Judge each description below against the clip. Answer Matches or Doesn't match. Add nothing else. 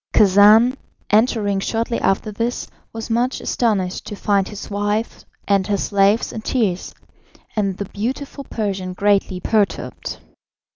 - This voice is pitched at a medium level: Doesn't match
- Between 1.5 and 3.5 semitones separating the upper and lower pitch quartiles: Matches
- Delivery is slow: Matches